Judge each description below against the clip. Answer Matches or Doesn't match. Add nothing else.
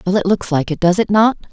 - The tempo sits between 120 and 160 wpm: Doesn't match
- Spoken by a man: Doesn't match